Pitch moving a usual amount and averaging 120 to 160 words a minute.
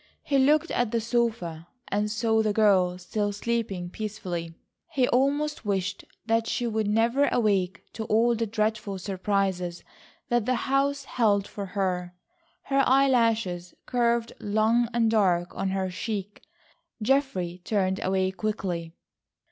Yes: average, 3.8 semitones; average, 140 wpm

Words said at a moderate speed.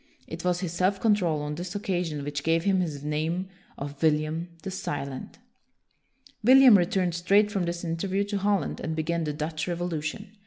Yes: average, 180 wpm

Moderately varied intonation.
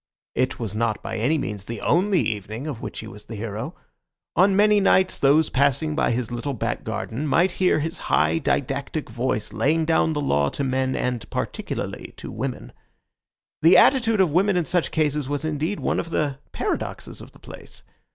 No: wide, 5.8 semitones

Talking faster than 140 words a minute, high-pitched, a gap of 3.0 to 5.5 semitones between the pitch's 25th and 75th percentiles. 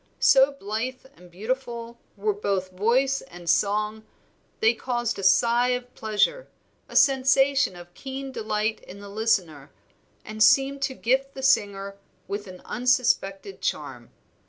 No: slow, 135 wpm; high, 225 Hz; average, 4.8 semitones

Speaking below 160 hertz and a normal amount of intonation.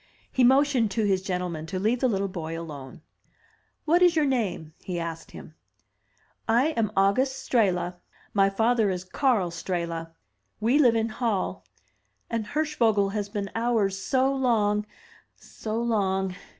No: high, 210 Hz; average, 4.6 semitones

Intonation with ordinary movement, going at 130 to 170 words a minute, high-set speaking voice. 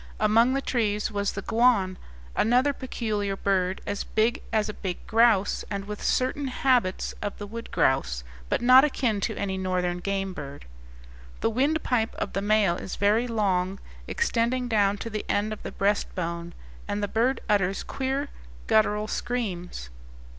Yes: average, 3.5 semitones; average, 160 wpm; high, 210 Hz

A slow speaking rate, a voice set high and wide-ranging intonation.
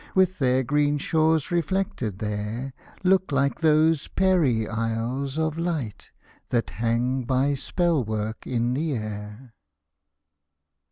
No: slow, 115 wpm; low, 135 Hz; wide, 5.8 semitones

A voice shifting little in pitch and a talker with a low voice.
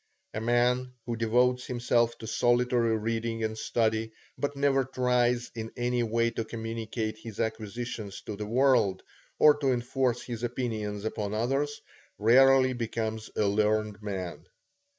Yes: narrow, 2.1 semitones; low, 115 Hz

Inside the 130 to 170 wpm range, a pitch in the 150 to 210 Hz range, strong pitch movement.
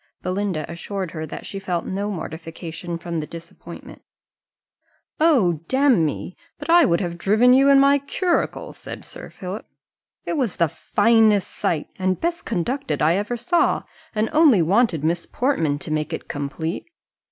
Yes: average, 155 wpm; high, 190 Hz; wide, 6.8 semitones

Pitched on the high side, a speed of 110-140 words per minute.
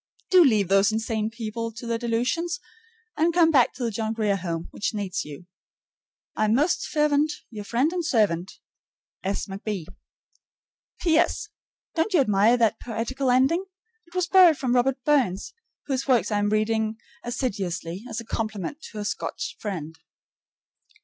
No: high, 230 Hz; average, 155 wpm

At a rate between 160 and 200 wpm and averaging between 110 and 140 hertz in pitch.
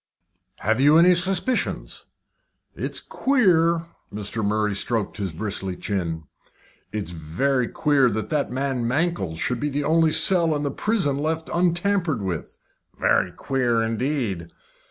No: slow, 135 wpm; low, 135 Hz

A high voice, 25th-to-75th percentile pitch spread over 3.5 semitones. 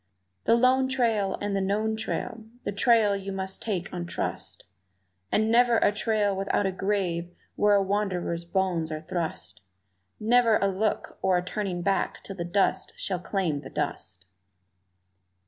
No: high, 195 Hz; average, 3.2 semitones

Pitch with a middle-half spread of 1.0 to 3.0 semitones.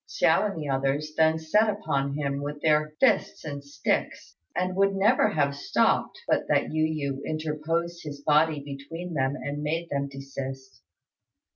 Yes: narrow, 2.6 semitones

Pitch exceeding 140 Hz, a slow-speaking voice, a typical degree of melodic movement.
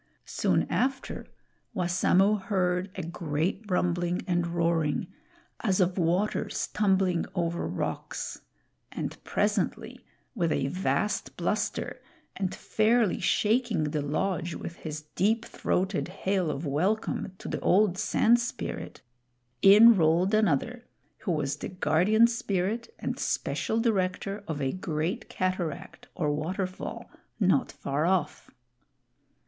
Yes: medium, 185 Hz; slow, 120 wpm; average, 3.8 semitones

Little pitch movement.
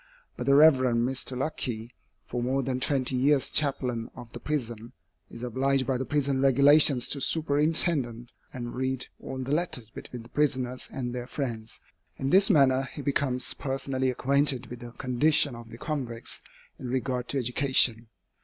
Yes: narrow, 2.3 semitones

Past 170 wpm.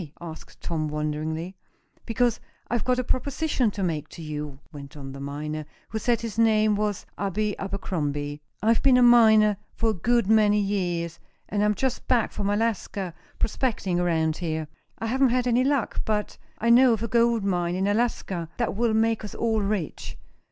Yes: average, 180 wpm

